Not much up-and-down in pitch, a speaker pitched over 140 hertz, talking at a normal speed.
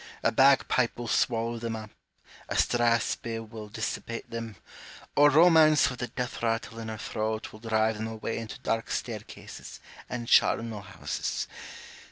No: narrow, 1.4 semitones; low, 115 Hz; average, 150 wpm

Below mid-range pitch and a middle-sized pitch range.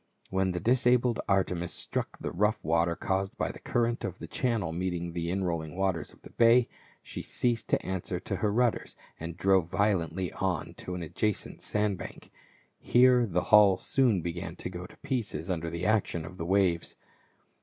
Yes: very low, 95 Hz; average, 3.9 semitones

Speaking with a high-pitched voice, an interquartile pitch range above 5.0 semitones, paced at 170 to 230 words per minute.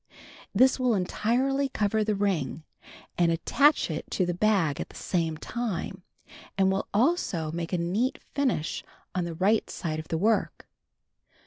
No: high, 195 Hz; wide, 5.6 semitones; average, 155 wpm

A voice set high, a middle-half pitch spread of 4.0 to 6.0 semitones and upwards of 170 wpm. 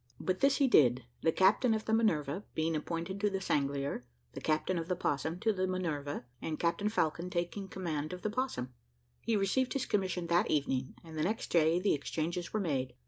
No: medium, 175 Hz; average, 4.4 semitones; fast, 205 wpm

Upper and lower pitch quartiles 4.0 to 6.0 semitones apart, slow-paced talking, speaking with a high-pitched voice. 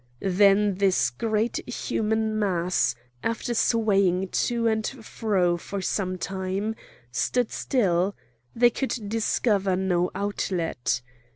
No: average, 3.3 semitones; slow, 105 wpm; high, 200 Hz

